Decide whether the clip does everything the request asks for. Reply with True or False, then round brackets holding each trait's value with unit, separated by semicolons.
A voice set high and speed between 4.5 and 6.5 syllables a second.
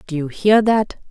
True (195 Hz; 4.7 syllables/s)